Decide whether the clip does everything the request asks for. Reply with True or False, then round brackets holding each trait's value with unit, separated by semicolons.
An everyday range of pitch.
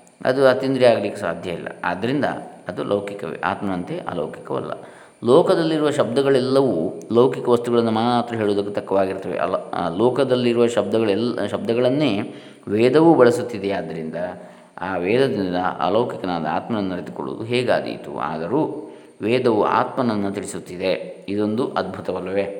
True (4.2 semitones)